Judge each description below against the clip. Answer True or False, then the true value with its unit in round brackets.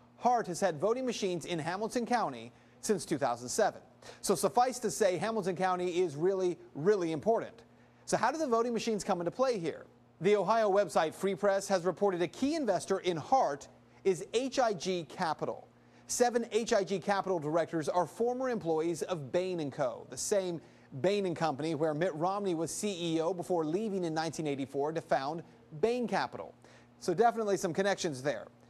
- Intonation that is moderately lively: True (4.4 semitones)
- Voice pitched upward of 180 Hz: True (190 Hz)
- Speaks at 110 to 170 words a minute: True (160 wpm)